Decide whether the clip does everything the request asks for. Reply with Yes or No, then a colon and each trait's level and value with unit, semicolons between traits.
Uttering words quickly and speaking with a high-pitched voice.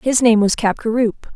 No: average, 180 wpm; high, 225 Hz